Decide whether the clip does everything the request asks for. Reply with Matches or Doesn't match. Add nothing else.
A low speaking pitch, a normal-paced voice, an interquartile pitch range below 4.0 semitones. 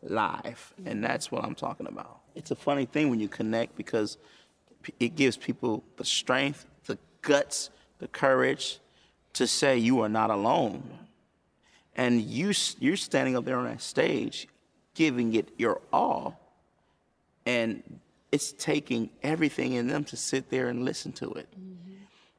Doesn't match